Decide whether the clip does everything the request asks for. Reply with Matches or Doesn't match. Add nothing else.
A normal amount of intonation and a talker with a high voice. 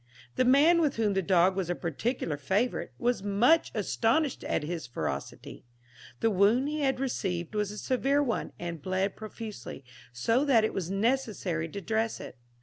Doesn't match